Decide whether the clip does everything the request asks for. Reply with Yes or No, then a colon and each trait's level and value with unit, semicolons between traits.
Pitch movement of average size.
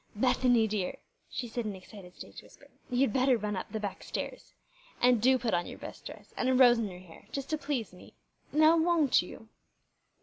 Yes: average, 4.1 semitones